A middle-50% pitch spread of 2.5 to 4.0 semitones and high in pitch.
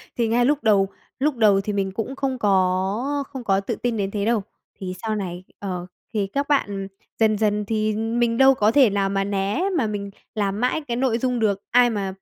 Yes: average, 3.6 semitones; high, 215 Hz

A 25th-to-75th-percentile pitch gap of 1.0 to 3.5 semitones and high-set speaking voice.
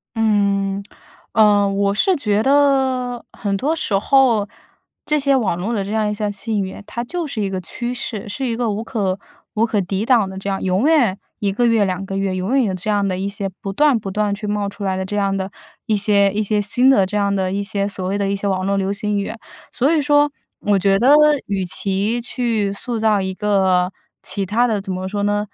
Yes: average, 2.8 semitones; high, 205 Hz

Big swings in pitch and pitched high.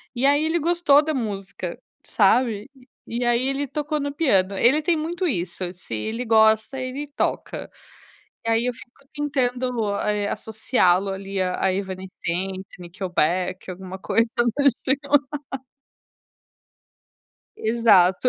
Yes: wide, 6.3 semitones; high, 225 Hz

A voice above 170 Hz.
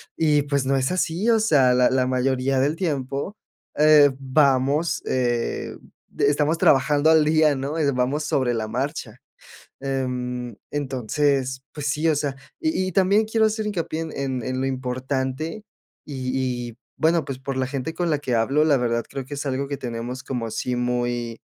No: low, 135 Hz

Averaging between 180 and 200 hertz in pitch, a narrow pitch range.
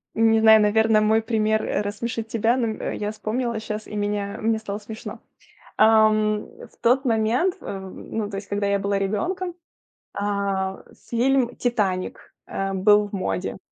No: high, 215 Hz; narrow, 1.8 semitones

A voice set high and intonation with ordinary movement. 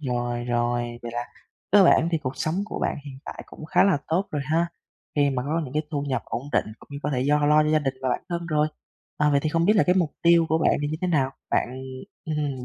No: medium, 150 Hz; average, 3.7 semitones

